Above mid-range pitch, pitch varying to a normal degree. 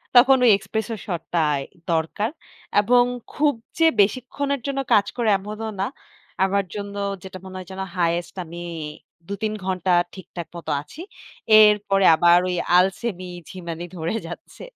Yes: high, 195 Hz; average, 4.1 semitones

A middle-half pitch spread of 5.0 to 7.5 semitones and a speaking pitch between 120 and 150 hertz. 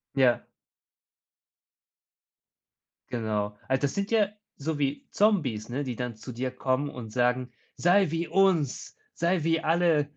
Yes: wide, 5.4 semitones; medium, 140 Hz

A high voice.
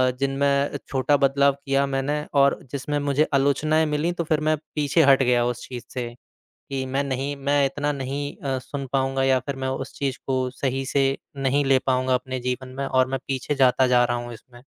No: low, 135 Hz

